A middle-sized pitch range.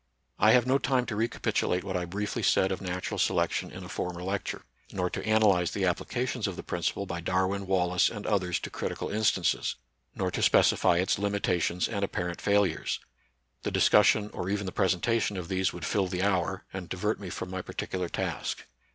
No: narrow, 2.3 semitones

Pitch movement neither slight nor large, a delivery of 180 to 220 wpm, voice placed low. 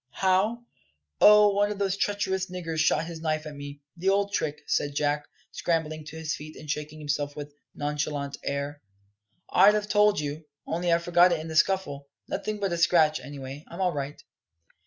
No: average, 4.4 semitones; average, 185 wpm; medium, 160 Hz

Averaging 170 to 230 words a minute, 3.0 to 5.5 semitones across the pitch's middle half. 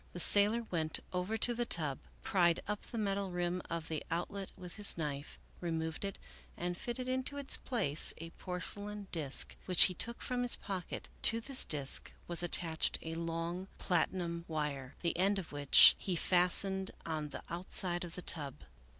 Yes: average, 175 wpm; average, 3.5 semitones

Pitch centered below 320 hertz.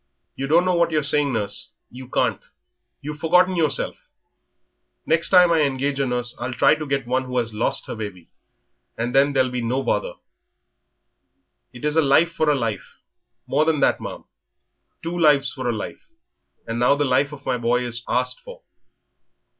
Yes: medium, 140 Hz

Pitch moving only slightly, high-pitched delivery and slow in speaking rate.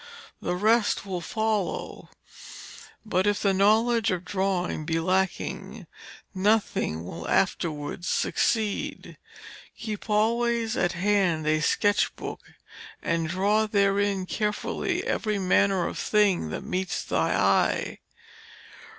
No: average, 3.1 semitones; high, 195 Hz; slow, 110 wpm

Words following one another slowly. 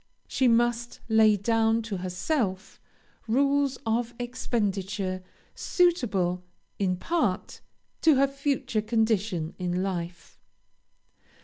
Yes: slow, 95 wpm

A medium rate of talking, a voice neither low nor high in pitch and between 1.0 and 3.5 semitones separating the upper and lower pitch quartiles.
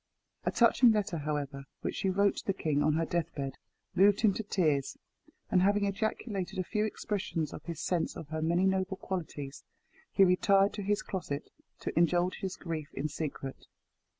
No: average, 180 wpm; medium, 180 Hz; average, 4.4 semitones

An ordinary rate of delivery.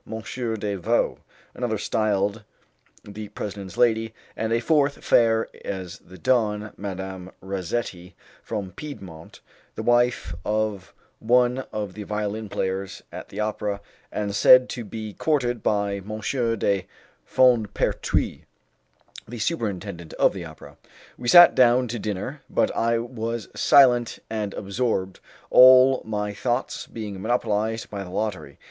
No: slow, 130 wpm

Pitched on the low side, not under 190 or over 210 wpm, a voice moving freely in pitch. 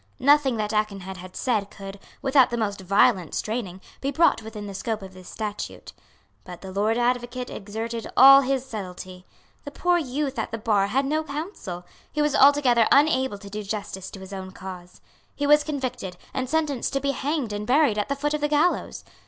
No: high, 230 Hz; average, 195 wpm; wide, 5.8 semitones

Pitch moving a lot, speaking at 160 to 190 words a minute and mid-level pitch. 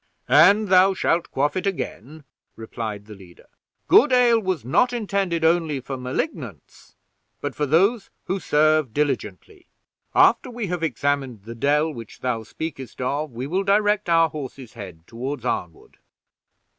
No: wide, 7.1 semitones; average, 145 wpm; medium, 150 Hz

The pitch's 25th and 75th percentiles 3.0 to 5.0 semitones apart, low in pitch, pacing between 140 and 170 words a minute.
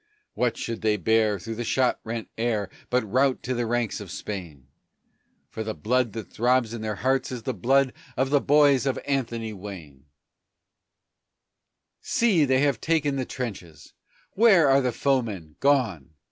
Yes: average, 4.0 semitones; low, 120 Hz; average, 160 wpm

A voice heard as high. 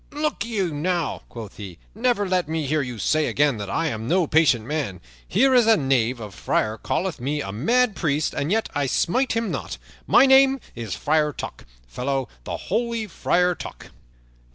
No: medium, 155 Hz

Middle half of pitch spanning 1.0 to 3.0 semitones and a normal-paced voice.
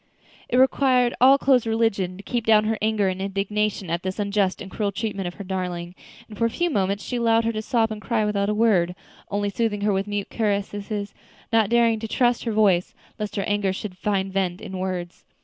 No: average, 2.7 semitones; fast, 220 wpm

